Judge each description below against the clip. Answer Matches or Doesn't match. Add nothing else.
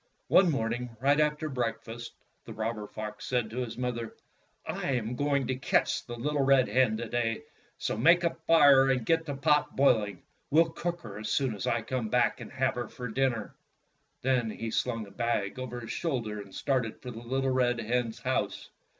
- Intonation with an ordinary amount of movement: Matches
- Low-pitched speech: Matches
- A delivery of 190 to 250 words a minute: Matches